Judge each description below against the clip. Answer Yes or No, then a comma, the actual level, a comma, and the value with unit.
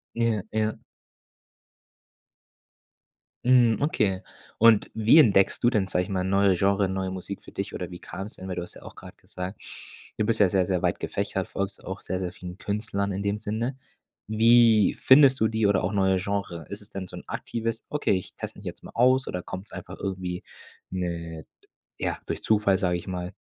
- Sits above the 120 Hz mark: No, low, 100 Hz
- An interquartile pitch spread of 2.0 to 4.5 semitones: Yes, average, 2.9 semitones